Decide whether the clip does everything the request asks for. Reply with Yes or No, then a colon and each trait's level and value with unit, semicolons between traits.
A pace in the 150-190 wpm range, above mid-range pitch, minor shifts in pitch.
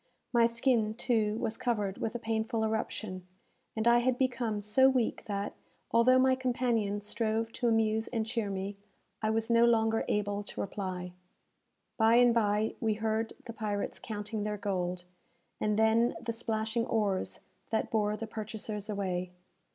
Yes: average, 160 wpm; high, 220 Hz; narrow, 1.9 semitones